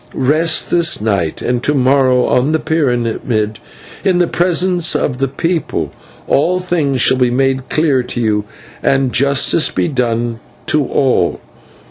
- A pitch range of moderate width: Yes, average, 4.4 semitones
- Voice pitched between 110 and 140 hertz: Yes, low, 135 Hz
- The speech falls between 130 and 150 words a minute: Yes, average, 145 wpm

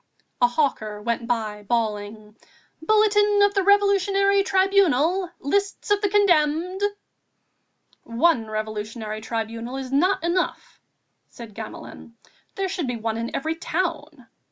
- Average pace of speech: No, slow, 120 wpm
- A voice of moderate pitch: No, very high, 295 Hz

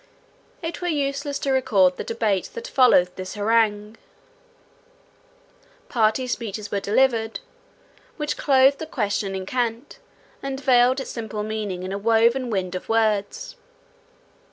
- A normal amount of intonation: Yes, average, 4.5 semitones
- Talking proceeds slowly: Yes, slow, 130 wpm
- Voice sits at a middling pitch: No, high, 225 Hz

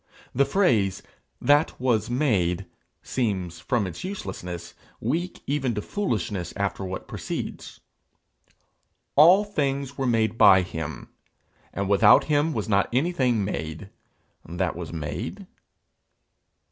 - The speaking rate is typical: No, slow, 115 wpm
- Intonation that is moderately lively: No, wide, 7.1 semitones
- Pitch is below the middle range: Yes, low, 110 Hz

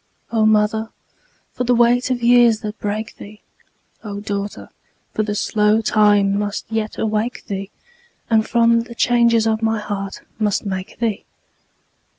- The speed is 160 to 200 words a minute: No, average, 145 wpm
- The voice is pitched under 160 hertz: No, high, 220 Hz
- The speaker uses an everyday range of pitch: No, narrow, 1.9 semitones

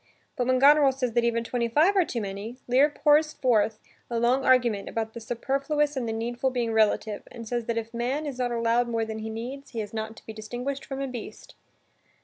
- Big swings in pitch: No, average, 3.0 semitones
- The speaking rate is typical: No, fast, 225 wpm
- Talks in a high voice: Yes, high, 240 Hz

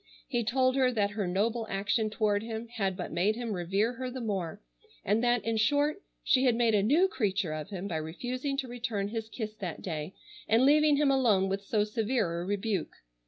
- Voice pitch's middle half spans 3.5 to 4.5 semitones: Yes, average, 3.8 semitones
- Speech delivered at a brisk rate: Yes, fast, 210 wpm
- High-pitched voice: Yes, high, 220 Hz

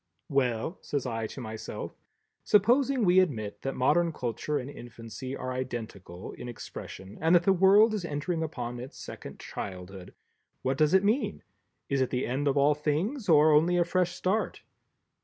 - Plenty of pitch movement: Yes, wide, 6.4 semitones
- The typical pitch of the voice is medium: Yes, medium, 145 Hz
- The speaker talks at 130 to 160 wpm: No, average, 170 wpm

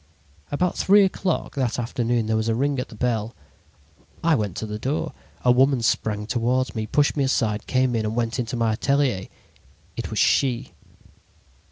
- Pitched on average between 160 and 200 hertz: No, low, 120 Hz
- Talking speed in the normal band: Yes, average, 180 wpm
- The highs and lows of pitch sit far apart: No, average, 3.4 semitones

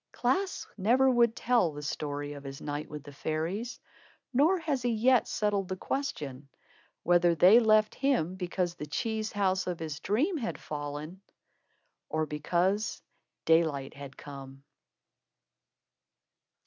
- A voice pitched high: No, medium, 180 Hz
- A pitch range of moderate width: No, wide, 7.4 semitones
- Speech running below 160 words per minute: Yes, slow, 135 wpm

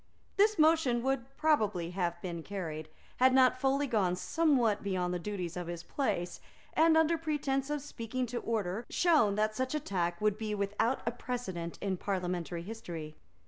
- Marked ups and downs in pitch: Yes, wide, 7.0 semitones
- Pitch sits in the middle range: No, high, 215 Hz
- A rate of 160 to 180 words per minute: Yes, average, 170 wpm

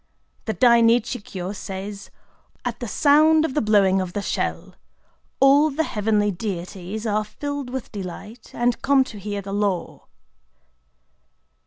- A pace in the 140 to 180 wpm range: Yes, average, 145 wpm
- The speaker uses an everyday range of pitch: Yes, average, 4.4 semitones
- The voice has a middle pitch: No, high, 215 Hz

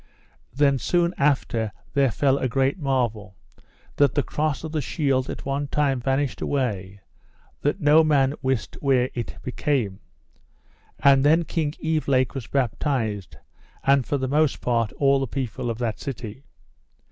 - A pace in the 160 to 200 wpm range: No, average, 150 wpm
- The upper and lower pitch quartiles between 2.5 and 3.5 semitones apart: Yes, average, 2.8 semitones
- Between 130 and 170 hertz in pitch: Yes, low, 135 Hz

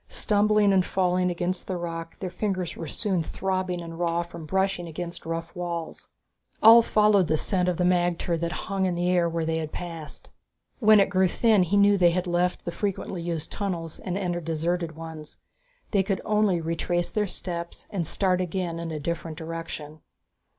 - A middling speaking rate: Yes, average, 190 wpm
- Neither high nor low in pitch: Yes, medium, 175 Hz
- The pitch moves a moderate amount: No, narrow, 2.3 semitones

